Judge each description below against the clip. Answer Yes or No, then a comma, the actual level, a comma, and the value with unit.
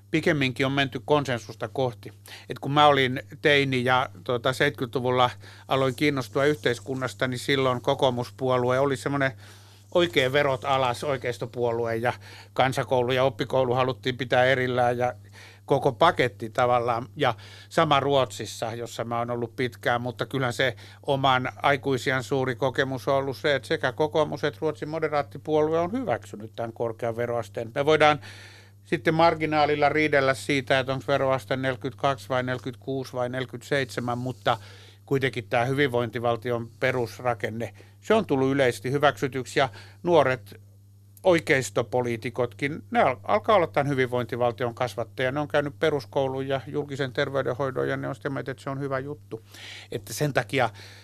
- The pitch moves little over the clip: No, average, 3.1 semitones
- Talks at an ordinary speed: Yes, average, 140 wpm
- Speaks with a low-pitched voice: Yes, low, 130 Hz